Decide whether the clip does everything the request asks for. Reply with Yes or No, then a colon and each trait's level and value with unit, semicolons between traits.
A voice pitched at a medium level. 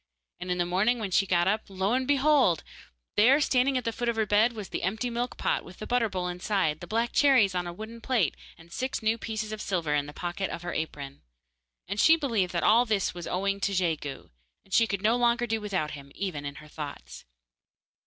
No: high, 200 Hz